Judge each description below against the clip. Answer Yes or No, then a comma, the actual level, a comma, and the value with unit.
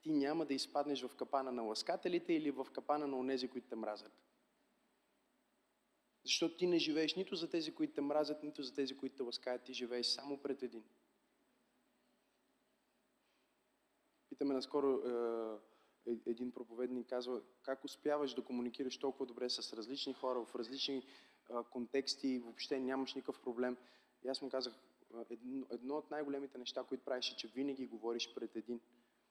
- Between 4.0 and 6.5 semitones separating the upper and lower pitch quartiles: No, narrow, 2.5 semitones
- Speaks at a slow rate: No, average, 160 wpm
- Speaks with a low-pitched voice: Yes, low, 130 Hz